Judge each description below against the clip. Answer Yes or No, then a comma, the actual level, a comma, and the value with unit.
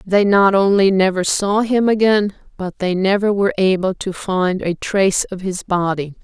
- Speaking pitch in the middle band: No, high, 195 Hz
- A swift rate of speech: No, average, 185 wpm